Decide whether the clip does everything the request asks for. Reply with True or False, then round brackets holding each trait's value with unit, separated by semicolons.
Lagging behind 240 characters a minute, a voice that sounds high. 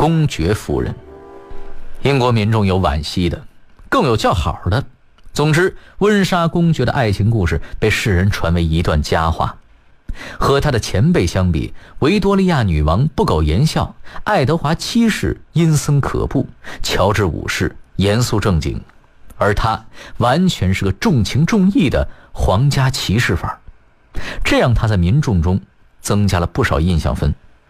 False (225 characters per minute; 105 Hz)